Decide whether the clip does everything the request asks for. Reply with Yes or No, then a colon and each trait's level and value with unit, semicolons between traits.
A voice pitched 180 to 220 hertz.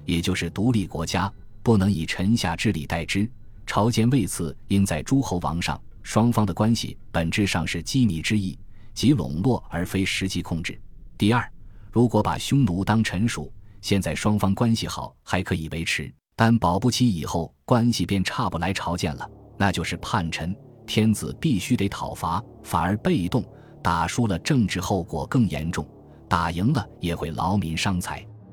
No: low, 100 Hz